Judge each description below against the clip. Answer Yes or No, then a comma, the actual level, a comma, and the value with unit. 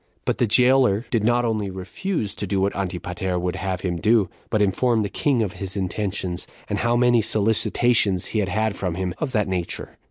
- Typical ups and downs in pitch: Yes, average, 3.8 semitones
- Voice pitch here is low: Yes, low, 100 Hz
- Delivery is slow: No, average, 195 wpm